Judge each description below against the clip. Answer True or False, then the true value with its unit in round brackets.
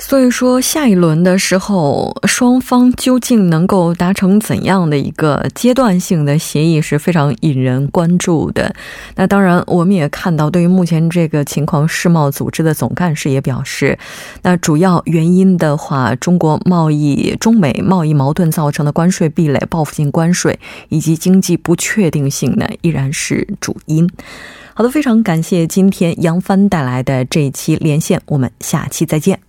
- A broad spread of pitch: False (3.8 semitones)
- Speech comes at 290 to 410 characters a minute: False (265 characters per minute)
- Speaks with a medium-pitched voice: True (170 Hz)